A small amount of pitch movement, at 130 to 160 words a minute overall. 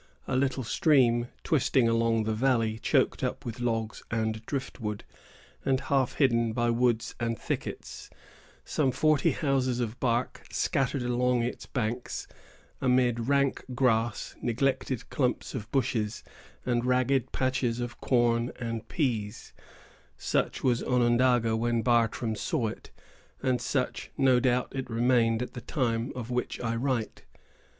Yes: narrow, 2.0 semitones; slow, 135 wpm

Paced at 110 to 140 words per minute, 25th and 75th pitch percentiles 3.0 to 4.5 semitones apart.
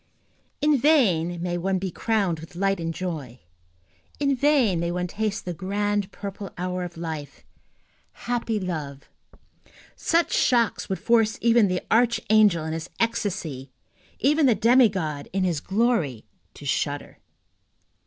No: slow, 135 wpm; average, 5.2 semitones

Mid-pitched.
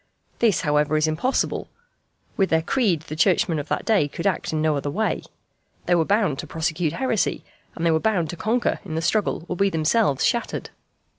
Yes: medium, 170 Hz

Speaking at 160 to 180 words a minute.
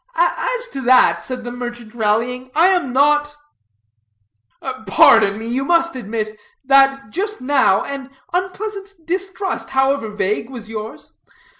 No: average, 140 wpm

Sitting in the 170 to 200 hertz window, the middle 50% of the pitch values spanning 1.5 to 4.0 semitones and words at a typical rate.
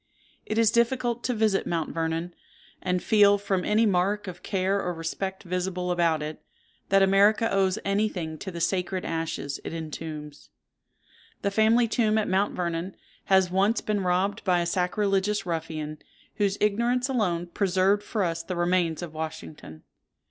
Yes: high, 190 Hz; average, 3.4 semitones; average, 160 wpm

